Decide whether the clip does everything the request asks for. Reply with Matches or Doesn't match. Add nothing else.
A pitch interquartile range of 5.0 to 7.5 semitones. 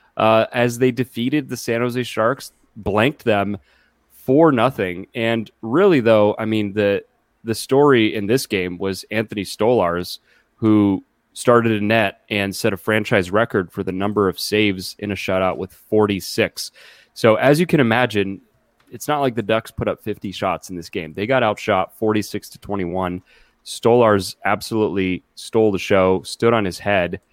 Doesn't match